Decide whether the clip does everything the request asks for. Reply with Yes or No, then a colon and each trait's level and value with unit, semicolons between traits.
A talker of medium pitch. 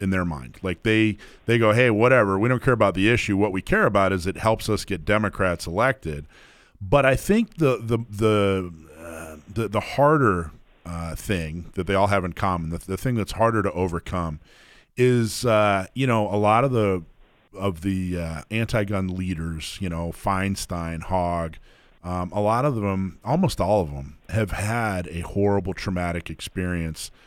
No: low, 100 Hz